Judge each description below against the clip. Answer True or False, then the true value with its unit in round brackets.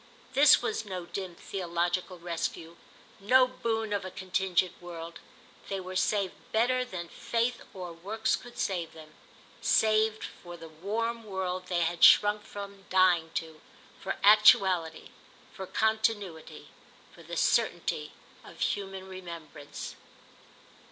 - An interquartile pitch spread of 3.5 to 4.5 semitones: True (3.8 semitones)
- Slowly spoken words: True (125 wpm)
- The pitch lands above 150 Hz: True (190 Hz)